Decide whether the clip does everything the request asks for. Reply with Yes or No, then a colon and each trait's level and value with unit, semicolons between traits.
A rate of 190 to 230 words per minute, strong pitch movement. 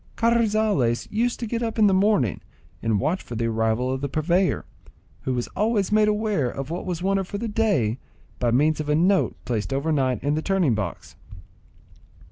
Yes: average, 195 wpm; wide, 8.6 semitones